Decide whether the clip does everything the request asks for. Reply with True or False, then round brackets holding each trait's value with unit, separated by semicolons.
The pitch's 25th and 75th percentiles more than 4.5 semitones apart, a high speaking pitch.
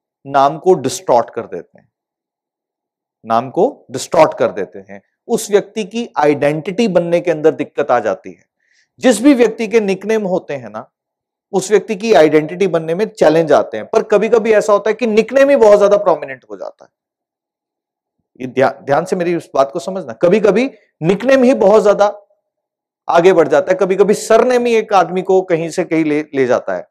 True (4.9 semitones; 200 Hz)